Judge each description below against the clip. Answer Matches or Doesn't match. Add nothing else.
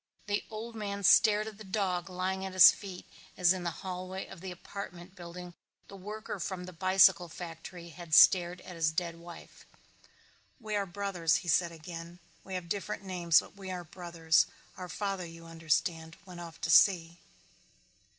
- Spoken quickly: Doesn't match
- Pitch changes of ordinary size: Doesn't match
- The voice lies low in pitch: Doesn't match